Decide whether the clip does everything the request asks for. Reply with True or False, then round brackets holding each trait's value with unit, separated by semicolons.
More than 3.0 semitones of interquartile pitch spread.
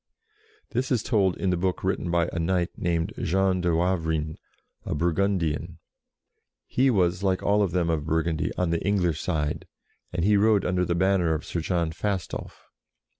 False (2.6 semitones)